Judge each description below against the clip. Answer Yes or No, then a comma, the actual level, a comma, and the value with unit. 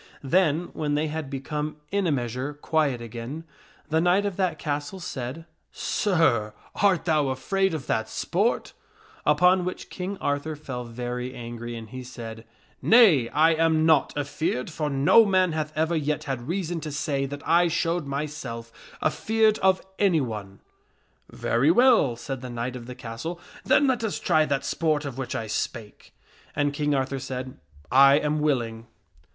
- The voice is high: No, medium, 145 Hz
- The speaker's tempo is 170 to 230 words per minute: Yes, average, 180 wpm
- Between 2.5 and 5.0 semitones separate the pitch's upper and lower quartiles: Yes, average, 4.6 semitones